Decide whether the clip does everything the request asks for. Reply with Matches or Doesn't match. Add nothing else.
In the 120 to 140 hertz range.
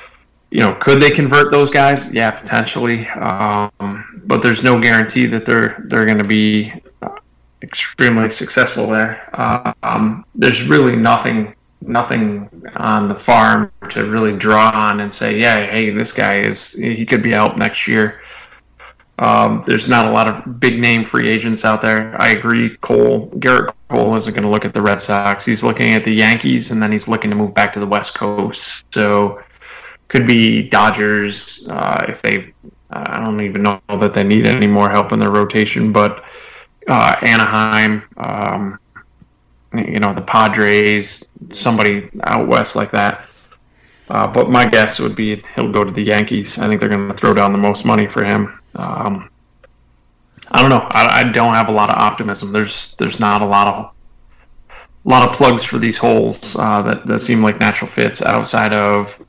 Doesn't match